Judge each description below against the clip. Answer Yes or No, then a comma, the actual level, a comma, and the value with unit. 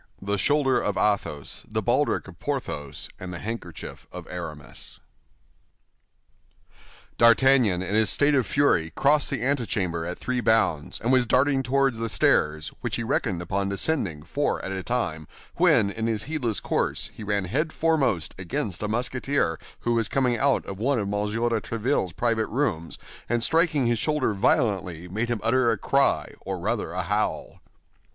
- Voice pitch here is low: Yes, low, 115 Hz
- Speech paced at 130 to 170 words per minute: Yes, average, 165 wpm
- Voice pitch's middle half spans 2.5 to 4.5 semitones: No, wide, 5.4 semitones